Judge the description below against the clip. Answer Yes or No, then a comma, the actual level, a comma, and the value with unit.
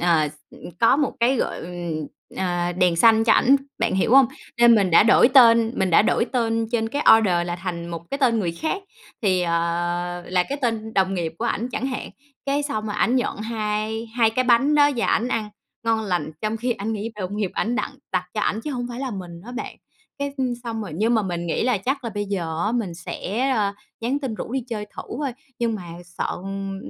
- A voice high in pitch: Yes, high, 220 Hz